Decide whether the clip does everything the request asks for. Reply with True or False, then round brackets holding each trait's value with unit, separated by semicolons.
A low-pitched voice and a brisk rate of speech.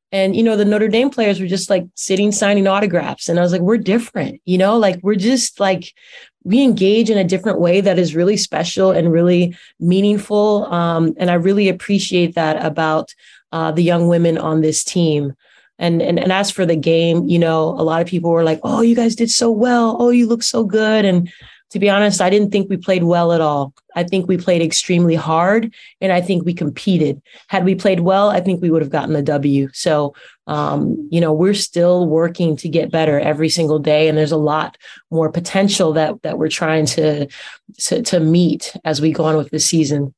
False (175 Hz; 220 wpm)